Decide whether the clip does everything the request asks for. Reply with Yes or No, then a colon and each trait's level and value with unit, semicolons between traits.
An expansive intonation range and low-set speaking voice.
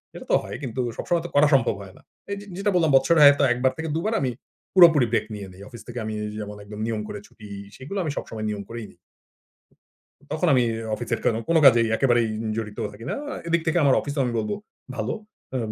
Yes: wide, 6.0 semitones; low, 125 Hz